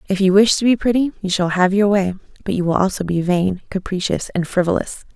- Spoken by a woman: Yes, female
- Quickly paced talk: Yes, fast, 235 wpm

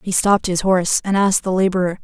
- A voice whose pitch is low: No, medium, 185 Hz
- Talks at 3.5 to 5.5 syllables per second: No, 6.8 syllables/s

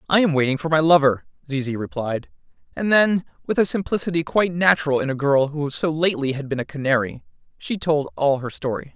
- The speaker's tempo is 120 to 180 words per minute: No, average, 200 wpm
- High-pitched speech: No, medium, 150 Hz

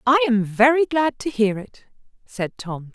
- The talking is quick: No, average, 185 wpm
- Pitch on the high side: Yes, high, 230 Hz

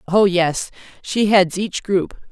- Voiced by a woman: Yes, female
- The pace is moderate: Yes, average, 155 wpm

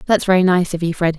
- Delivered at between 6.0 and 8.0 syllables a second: Yes, 7.9 syllables/s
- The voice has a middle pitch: Yes, medium, 180 Hz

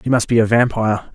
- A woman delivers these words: No, male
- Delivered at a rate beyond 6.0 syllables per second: Yes, 6.4 syllables/s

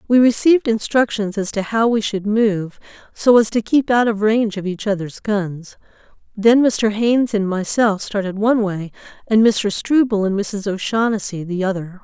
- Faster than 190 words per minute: No, average, 180 wpm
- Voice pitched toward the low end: No, high, 210 Hz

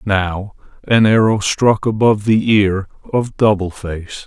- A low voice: Yes, low, 105 Hz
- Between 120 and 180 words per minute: Yes, average, 140 wpm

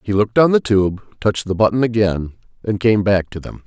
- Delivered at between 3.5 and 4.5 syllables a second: No, 5.5 syllables/s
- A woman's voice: No, male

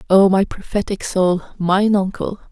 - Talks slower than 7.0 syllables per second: Yes, 4.3 syllables/s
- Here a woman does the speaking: Yes, female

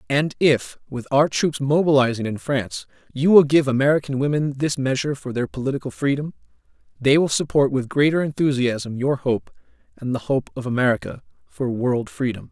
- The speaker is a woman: No, male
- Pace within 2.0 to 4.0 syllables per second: No, 5.4 syllables/s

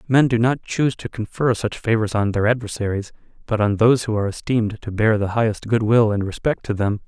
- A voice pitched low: Yes, low, 110 Hz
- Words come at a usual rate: No, fast, 230 wpm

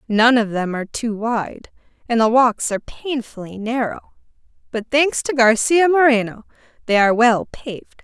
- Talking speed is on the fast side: No, average, 155 wpm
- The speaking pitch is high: Yes, high, 235 Hz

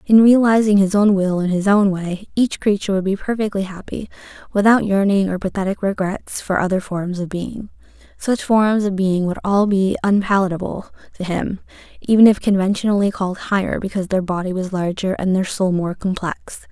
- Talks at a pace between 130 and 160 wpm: No, average, 180 wpm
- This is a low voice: No, high, 195 Hz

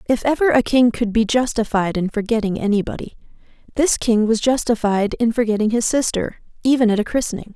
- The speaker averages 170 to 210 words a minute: Yes, average, 175 wpm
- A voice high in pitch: Yes, high, 225 Hz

